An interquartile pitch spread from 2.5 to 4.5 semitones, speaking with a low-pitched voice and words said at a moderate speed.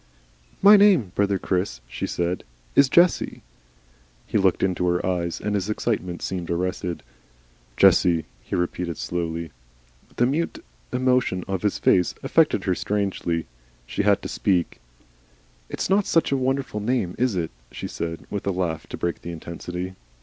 No: wide, 5.4 semitones; very low, 95 Hz; average, 155 wpm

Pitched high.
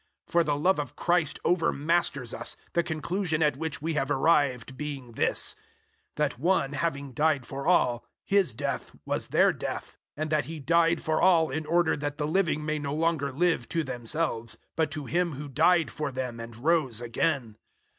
No: medium, 150 Hz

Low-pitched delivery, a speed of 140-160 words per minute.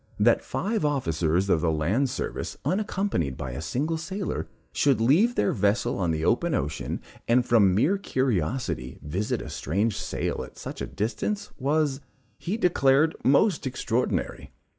Yes: low, 125 Hz; average, 150 wpm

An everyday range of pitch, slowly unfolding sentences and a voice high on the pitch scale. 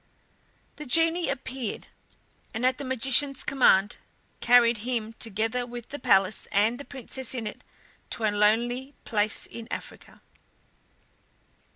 Yes: average, 3.2 semitones; slow, 130 wpm; high, 240 Hz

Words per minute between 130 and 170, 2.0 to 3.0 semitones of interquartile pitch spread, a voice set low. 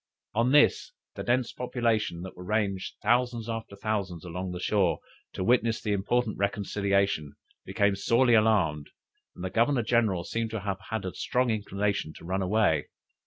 No: average, 165 wpm; average, 3.5 semitones; low, 105 Hz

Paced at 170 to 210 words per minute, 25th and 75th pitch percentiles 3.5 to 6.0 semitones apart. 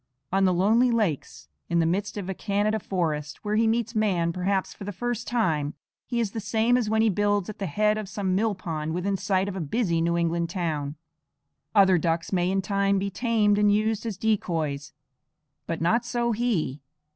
Yes: fast, 205 wpm; average, 4.1 semitones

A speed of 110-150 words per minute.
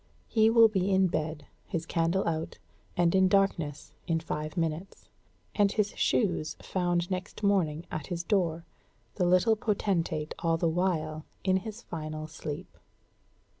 Yes: average, 145 wpm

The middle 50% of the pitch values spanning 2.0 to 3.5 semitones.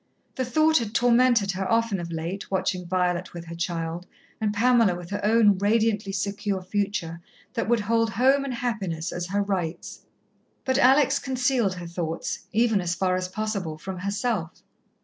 No: average, 4.4 semitones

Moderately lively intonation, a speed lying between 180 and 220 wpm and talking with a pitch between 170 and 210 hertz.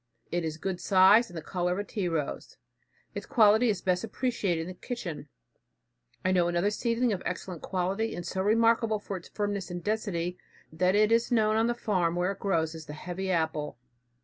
Yes: average, 3.7 semitones; average, 200 wpm; high, 190 Hz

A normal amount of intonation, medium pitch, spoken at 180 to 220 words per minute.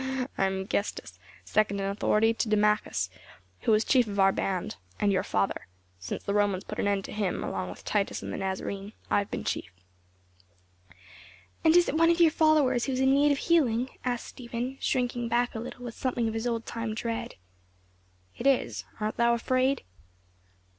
No: average, 4.1 semitones; high, 230 Hz; average, 190 wpm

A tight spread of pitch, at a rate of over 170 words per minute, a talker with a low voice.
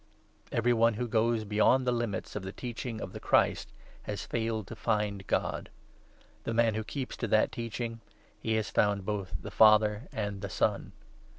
Yes: narrow, 1.9 semitones; average, 190 wpm; low, 110 Hz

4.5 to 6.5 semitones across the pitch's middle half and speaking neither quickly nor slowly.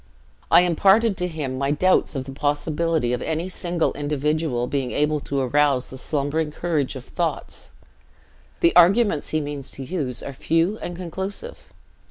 No: average, 3.8 semitones; average, 160 wpm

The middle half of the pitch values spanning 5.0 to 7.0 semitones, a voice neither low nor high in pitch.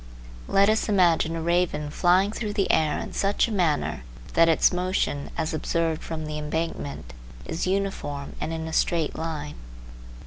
No: average, 3.0 semitones; medium, 165 Hz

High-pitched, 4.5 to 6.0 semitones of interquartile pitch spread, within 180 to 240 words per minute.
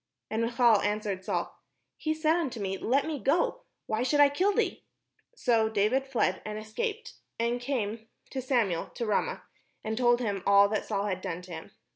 Yes: high, 230 Hz; average, 4.8 semitones; average, 185 wpm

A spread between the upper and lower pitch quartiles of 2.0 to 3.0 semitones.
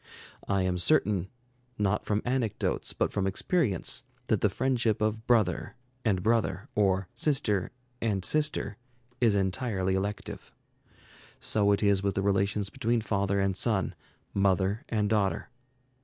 Yes: narrow, 2.6 semitones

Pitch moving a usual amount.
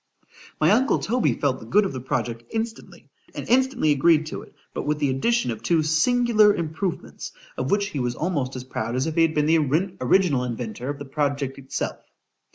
No: wide, 6.7 semitones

